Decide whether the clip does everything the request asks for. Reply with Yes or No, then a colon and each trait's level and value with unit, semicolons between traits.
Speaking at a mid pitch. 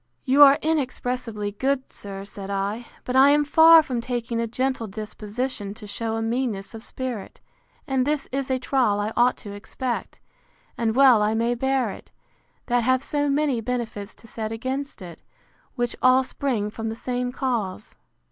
No: high, 240 Hz